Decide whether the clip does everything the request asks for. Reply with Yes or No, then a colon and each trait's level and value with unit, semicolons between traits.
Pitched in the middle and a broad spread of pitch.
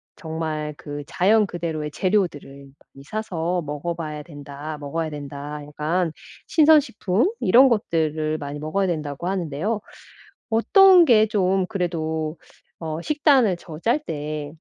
No: medium, 165 Hz; average, 4.9 semitones